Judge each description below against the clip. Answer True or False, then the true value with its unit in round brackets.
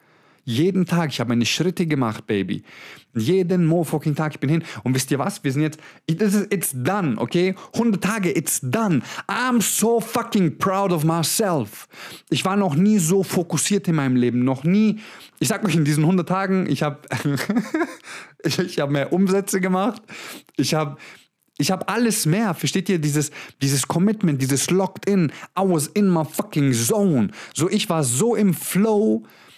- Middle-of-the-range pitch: True (175 Hz)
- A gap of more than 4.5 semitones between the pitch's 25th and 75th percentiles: True (4.9 semitones)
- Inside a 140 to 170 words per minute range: False (180 wpm)